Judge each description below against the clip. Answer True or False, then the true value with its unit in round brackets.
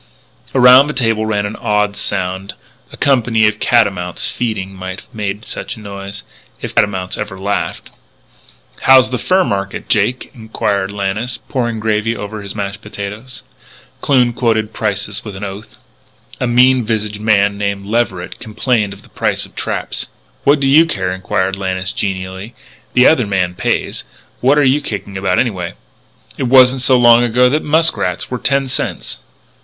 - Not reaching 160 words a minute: False (165 wpm)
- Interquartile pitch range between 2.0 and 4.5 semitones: True (4.0 semitones)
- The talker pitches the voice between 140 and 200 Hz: False (105 Hz)